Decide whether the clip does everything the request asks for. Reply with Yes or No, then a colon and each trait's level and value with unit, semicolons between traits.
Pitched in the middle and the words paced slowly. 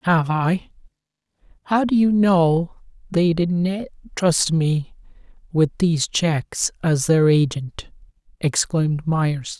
Yes: medium, 165 Hz; slow, 115 wpm